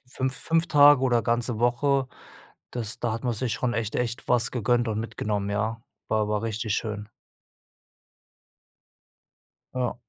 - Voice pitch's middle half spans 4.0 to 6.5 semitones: No, narrow, 2.5 semitones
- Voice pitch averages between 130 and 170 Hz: No, low, 120 Hz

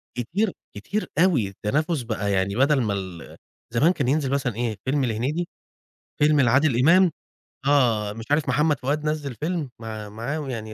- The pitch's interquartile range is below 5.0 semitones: No, wide, 5.4 semitones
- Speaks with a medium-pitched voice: No, low, 130 Hz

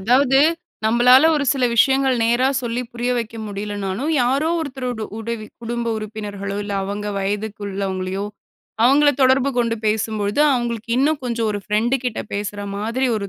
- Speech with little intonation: No, average, 3.8 semitones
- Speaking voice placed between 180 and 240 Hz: Yes, high, 230 Hz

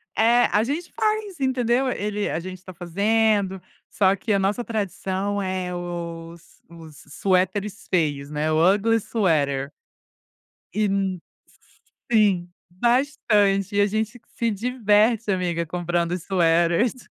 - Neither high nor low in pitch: No, high, 195 Hz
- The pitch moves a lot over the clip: No, average, 4.1 semitones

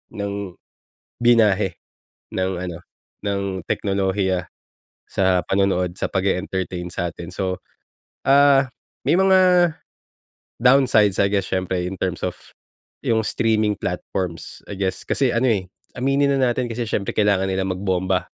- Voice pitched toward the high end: No, low, 100 Hz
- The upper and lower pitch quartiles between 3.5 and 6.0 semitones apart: Yes, average, 4.2 semitones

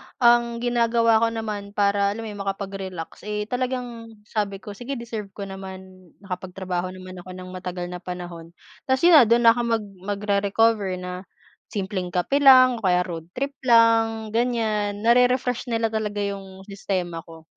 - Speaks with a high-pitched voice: Yes, high, 205 Hz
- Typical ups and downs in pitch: Yes, average, 3.7 semitones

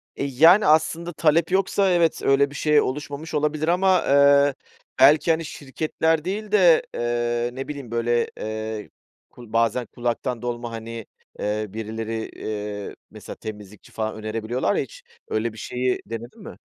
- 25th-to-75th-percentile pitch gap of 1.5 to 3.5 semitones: No, wide, 5.5 semitones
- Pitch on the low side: Yes, low, 130 Hz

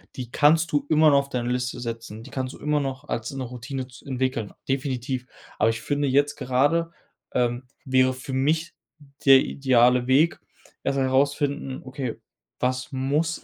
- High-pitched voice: No, low, 130 Hz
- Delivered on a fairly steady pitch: Yes, narrow, 2.2 semitones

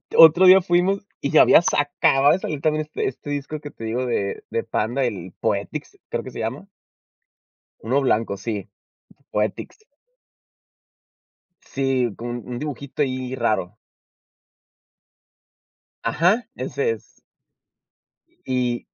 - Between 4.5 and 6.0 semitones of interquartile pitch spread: Yes, average, 4.8 semitones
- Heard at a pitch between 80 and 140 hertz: Yes, low, 135 Hz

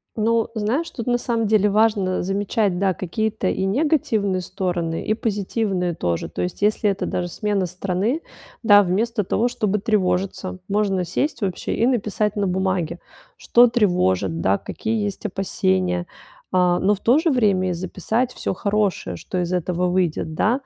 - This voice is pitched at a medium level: No, high, 195 Hz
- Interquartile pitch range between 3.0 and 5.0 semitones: Yes, average, 3.3 semitones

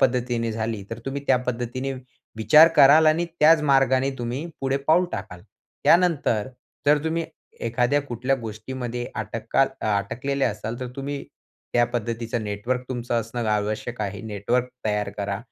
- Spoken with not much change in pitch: No, average, 3.6 semitones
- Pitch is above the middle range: No, low, 120 Hz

